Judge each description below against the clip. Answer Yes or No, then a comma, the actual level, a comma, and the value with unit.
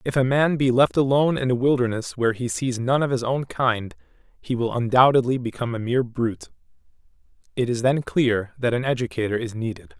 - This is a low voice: Yes, low, 125 Hz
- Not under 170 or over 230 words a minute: Yes, average, 200 wpm